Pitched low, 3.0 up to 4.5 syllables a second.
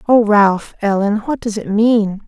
No: high, 210 Hz; 4.0 syllables/s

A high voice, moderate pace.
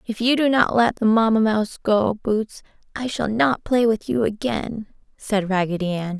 Yes: high, 220 Hz; average, 195 wpm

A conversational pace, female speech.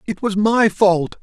No: average, 195 wpm; male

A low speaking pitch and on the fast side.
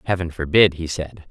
No: very low, 85 Hz; average, 185 wpm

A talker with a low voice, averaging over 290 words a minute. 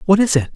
No: medium, 185 Hz; fast, 325 wpm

